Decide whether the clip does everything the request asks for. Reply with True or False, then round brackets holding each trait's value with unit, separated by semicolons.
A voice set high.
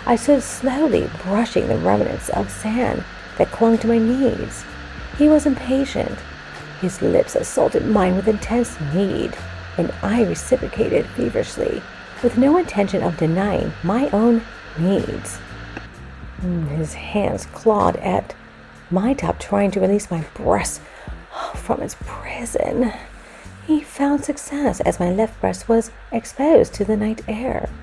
True (220 Hz)